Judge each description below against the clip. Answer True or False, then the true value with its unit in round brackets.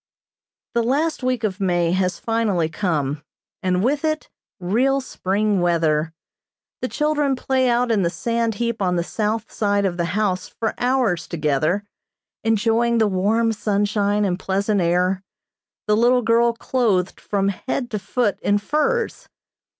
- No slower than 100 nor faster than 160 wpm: True (150 wpm)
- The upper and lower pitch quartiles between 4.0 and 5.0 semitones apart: True (4.3 semitones)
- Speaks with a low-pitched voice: False (210 Hz)